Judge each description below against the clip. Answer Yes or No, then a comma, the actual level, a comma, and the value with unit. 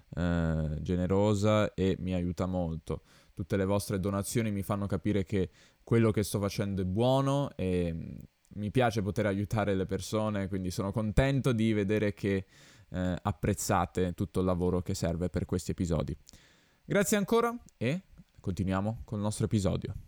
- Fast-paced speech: No, average, 150 wpm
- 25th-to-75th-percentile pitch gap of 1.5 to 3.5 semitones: Yes, average, 2.9 semitones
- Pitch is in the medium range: No, low, 100 Hz